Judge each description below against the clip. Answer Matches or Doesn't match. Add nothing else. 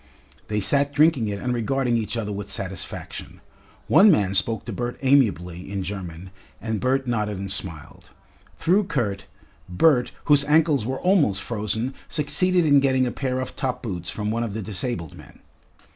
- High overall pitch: Doesn't match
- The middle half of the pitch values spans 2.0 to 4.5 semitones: Doesn't match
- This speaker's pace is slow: Doesn't match